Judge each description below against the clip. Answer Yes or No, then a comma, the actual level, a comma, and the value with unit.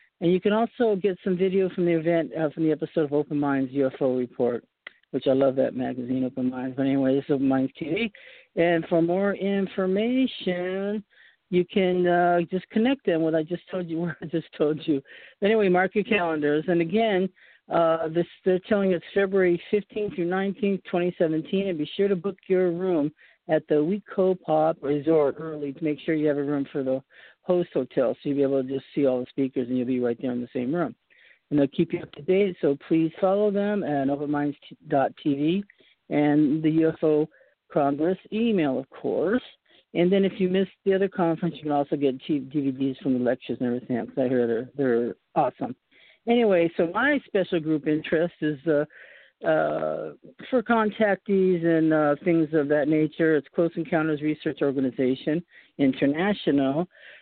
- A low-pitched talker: No, medium, 165 Hz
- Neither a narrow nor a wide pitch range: Yes, average, 4.6 semitones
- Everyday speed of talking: Yes, average, 190 wpm